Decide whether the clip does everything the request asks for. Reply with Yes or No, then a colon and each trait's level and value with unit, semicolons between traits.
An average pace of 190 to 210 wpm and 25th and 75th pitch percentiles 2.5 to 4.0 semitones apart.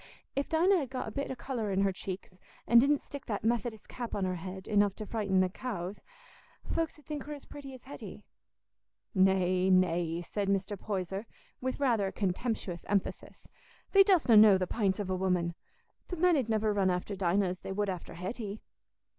No: average, 195 wpm; average, 5.0 semitones